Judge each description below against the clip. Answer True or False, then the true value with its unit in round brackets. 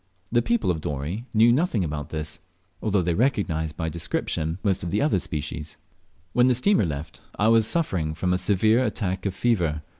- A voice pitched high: False (95 Hz)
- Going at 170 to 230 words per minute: True (185 wpm)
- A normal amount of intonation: False (6.2 semitones)